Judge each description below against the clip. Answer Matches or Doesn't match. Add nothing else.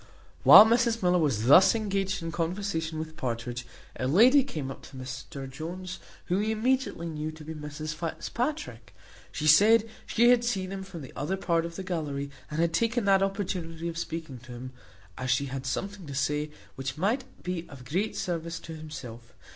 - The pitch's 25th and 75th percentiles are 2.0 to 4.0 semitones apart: Doesn't match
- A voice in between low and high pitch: Matches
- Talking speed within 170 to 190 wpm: Matches